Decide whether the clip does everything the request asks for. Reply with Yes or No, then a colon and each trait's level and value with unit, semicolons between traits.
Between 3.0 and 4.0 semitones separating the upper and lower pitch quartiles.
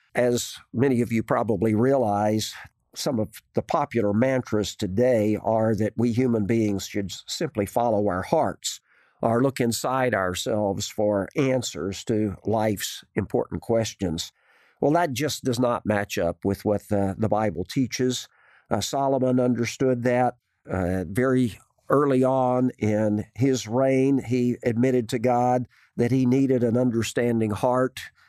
Yes: average, 3.3 semitones